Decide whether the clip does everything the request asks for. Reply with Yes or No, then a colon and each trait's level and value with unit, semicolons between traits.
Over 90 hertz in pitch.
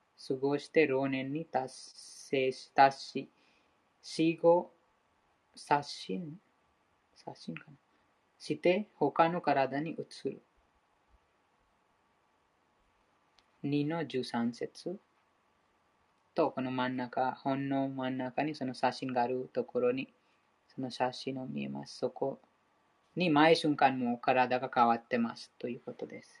Yes: low, 135 Hz